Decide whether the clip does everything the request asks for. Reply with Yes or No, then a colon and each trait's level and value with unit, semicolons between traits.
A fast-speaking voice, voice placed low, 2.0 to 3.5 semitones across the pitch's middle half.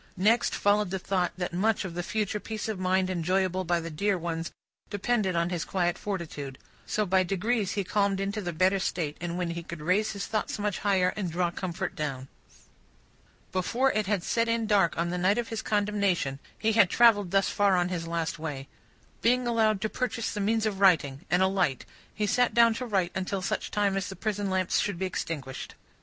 No: fast, 210 wpm; high, 190 Hz; average, 3.2 semitones